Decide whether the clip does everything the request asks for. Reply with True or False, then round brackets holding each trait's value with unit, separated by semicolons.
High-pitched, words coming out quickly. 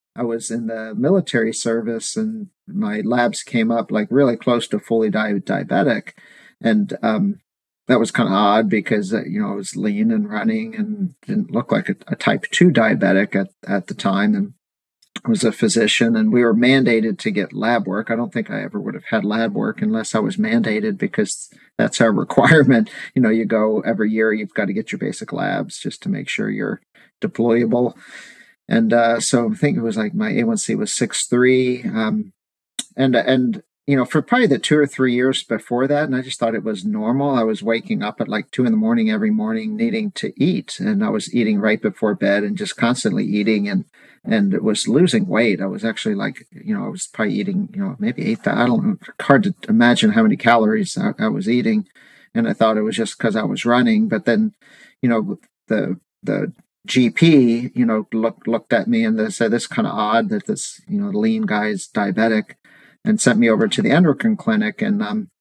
True (195 Hz; 215 wpm)